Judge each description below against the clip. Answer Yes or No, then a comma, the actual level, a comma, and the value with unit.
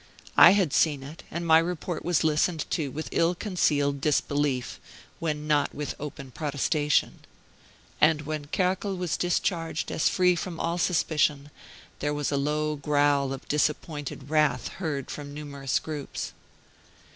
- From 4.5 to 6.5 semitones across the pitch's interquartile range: No, narrow, 2.5 semitones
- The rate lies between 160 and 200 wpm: No, average, 145 wpm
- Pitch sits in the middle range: Yes, medium, 150 Hz